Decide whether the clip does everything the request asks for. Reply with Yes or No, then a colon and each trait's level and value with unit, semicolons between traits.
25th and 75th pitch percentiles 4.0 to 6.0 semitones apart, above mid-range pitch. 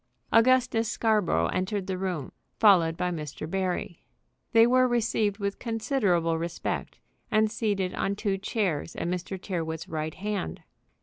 Yes: average, 4.5 semitones; high, 195 Hz